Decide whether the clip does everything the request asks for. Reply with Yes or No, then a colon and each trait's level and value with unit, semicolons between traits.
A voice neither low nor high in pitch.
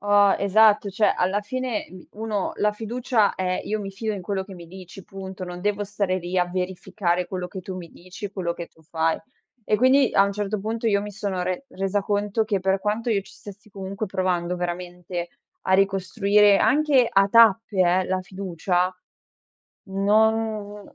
No: high, 195 Hz